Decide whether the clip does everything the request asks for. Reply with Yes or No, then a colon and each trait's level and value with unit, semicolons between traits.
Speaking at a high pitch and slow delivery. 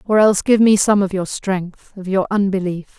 No: high, 195 Hz; average, 200 wpm